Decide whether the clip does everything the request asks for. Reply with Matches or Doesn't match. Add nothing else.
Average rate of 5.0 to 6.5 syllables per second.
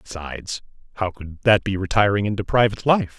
Matches